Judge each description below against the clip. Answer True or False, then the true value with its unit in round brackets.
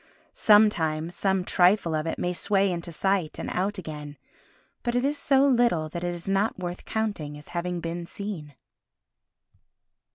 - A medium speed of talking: True (160 wpm)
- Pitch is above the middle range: False (180 Hz)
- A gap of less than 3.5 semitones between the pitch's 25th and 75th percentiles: False (3.9 semitones)